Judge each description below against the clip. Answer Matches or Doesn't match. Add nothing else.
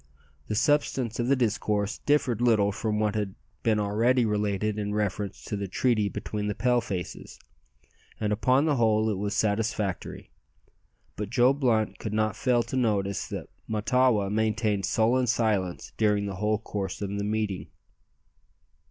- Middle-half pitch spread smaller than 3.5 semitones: Matches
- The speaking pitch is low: Matches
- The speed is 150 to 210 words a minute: Matches